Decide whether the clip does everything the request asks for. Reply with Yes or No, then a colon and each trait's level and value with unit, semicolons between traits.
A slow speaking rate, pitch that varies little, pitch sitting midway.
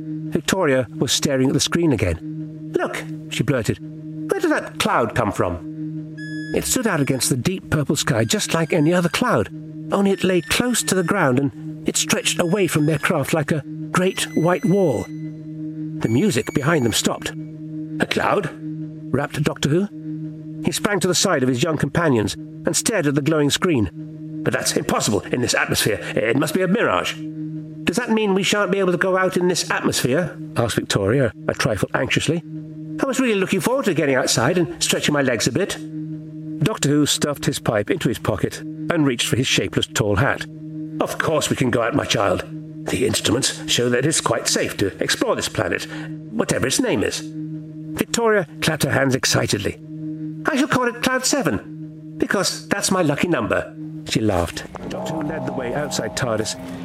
No: average, 190 wpm; narrow, 2.1 semitones; medium, 155 Hz